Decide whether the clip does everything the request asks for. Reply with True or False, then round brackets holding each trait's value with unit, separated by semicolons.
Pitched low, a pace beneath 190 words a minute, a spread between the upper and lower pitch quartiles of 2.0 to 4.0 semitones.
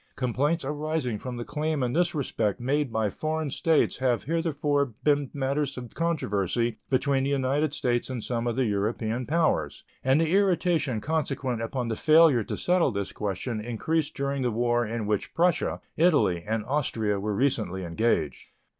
False (130 Hz; 165 wpm; 4.9 semitones)